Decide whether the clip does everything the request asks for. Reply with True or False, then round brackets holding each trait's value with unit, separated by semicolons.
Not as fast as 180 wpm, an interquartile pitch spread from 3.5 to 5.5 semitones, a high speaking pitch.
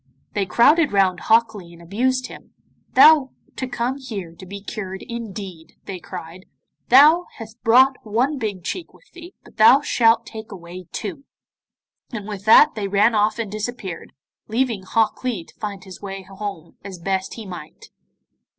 True (170 wpm; 4.2 semitones; 210 Hz)